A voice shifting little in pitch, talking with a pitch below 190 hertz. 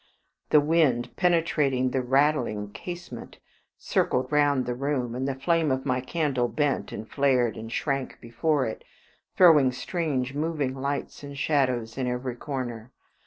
No: average, 3.0 semitones; low, 135 Hz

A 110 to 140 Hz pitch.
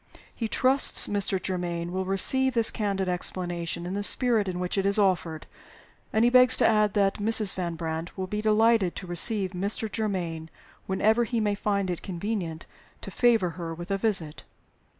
No: high, 195 Hz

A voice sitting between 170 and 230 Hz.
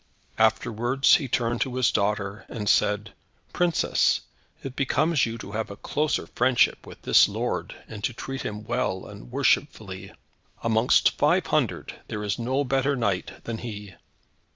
No: low, 115 Hz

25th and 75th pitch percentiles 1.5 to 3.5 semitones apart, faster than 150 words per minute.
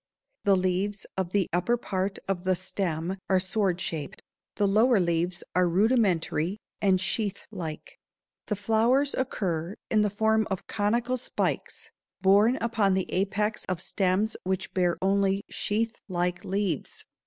No: average, 2.7 semitones; average, 140 wpm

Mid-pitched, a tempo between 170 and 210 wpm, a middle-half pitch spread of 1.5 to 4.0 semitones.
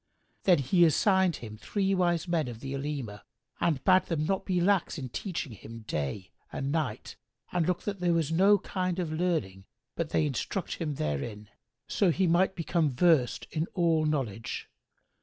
No: medium, 160 Hz; average, 175 wpm; wide, 5.5 semitones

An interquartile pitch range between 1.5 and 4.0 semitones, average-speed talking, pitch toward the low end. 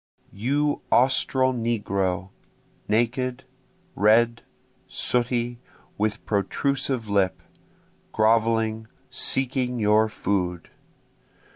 No: average, 3.0 semitones; slow, 70 wpm; low, 115 Hz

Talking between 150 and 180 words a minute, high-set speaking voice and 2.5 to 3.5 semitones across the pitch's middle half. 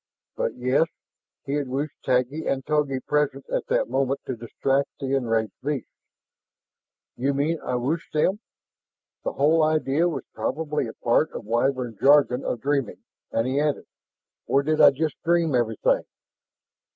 No: average, 155 wpm; medium, 140 Hz; average, 3.0 semitones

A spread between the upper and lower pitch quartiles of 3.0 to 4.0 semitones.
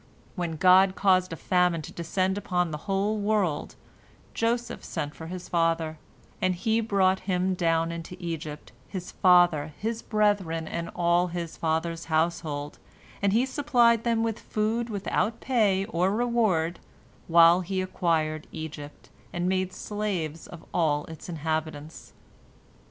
Yes: average, 3.7 semitones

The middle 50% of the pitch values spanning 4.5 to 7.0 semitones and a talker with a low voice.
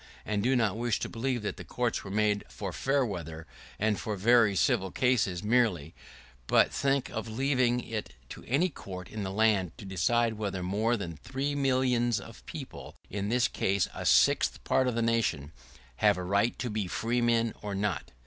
No: average, 3.6 semitones; low, 110 Hz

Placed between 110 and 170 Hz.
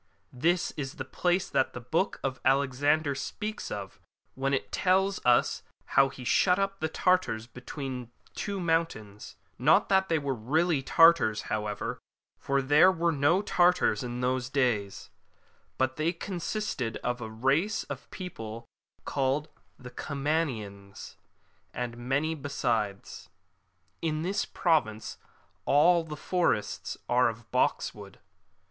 Yes: medium, 140 Hz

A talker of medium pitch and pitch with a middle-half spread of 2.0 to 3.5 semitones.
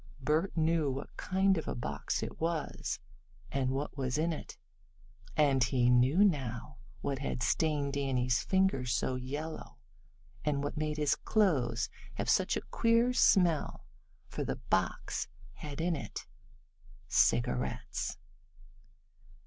No: medium, 145 Hz; average, 4.1 semitones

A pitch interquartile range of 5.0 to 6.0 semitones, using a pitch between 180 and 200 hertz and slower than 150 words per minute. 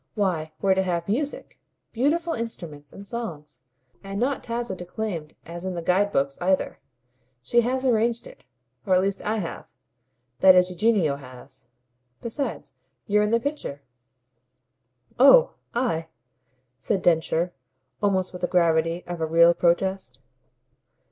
Yes: average, 5.3 semitones; medium, 185 Hz; average, 140 wpm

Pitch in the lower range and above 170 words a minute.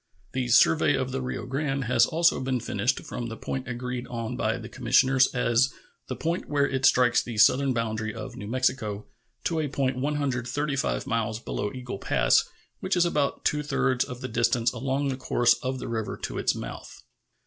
Yes: low, 130 Hz; average, 190 wpm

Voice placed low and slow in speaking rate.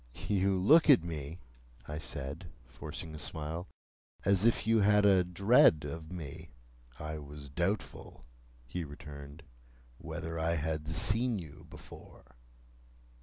Yes: very low, 80 Hz; slow, 125 wpm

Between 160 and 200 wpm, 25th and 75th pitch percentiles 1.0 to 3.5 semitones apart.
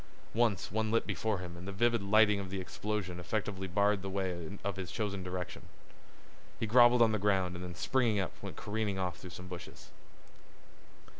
Yes: average, 190 wpm; average, 2.9 semitones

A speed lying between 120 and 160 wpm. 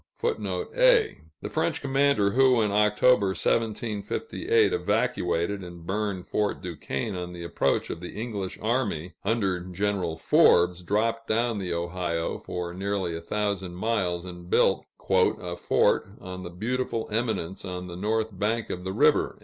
Yes: average, 150 wpm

